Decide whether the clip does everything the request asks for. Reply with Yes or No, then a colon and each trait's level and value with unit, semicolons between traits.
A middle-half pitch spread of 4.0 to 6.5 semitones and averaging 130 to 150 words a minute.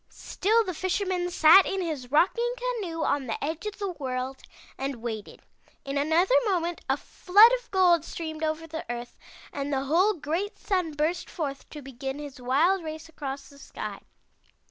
No: average, 5.0 semitones; average, 170 wpm